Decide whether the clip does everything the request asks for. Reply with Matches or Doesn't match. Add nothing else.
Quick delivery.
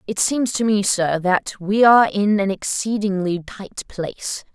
Doesn't match